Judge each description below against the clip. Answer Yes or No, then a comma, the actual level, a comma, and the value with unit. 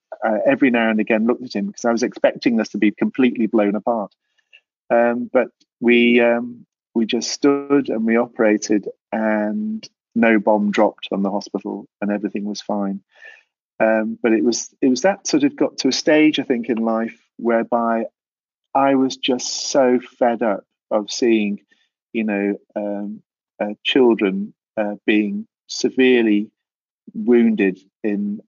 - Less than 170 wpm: Yes, average, 160 wpm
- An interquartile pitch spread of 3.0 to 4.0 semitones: No, narrow, 2.6 semitones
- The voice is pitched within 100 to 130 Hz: Yes, low, 115 Hz